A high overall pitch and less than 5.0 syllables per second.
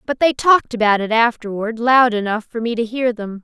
No: high, 230 Hz; 5.4 syllables/s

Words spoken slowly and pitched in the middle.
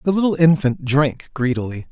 No: average, 155 wpm; medium, 145 Hz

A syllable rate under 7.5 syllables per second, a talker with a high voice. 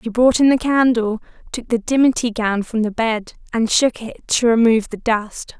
Yes: 4.8 syllables/s; high, 230 Hz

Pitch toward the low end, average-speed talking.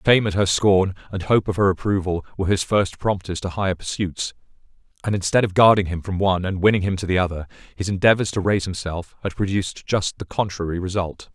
No: very low, 95 Hz; fast, 210 wpm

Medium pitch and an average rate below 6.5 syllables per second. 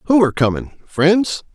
Yes: medium, 165 Hz; 5.0 syllables/s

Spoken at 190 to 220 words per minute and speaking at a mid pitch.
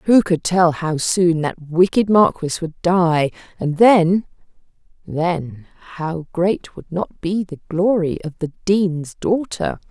No: average, 140 wpm; medium, 175 Hz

